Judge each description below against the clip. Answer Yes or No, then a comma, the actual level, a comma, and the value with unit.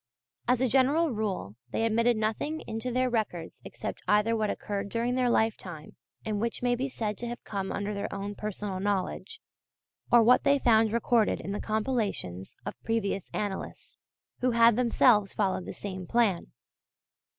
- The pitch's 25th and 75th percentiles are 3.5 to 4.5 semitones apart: No, average, 3.1 semitones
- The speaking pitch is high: Yes, high, 220 Hz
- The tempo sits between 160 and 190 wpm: Yes, average, 165 wpm